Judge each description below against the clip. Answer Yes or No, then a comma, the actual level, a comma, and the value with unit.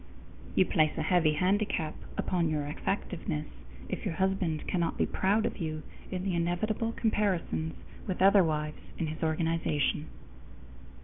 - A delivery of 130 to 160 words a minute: Yes, average, 145 wpm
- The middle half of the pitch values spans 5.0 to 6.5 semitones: No, average, 3.4 semitones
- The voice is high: No, medium, 170 Hz